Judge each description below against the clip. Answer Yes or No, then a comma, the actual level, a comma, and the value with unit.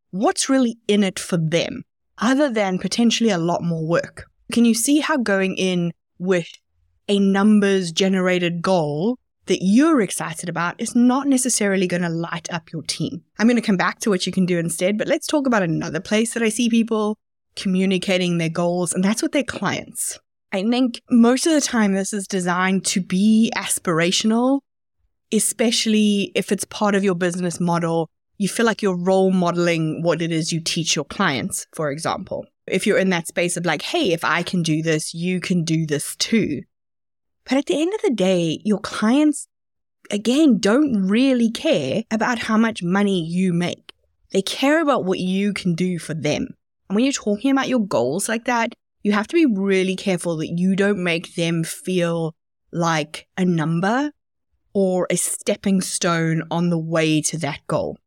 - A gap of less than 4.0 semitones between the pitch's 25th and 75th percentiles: No, average, 4.7 semitones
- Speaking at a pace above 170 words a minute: Yes, average, 185 wpm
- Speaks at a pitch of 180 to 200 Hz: Yes, high, 190 Hz